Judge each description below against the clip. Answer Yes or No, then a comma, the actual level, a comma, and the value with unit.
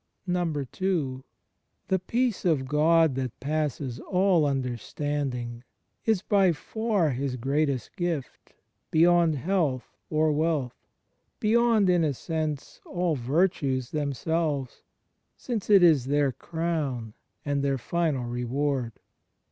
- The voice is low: No, medium, 150 Hz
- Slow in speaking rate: Yes, slow, 110 wpm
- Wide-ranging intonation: No, average, 4.6 semitones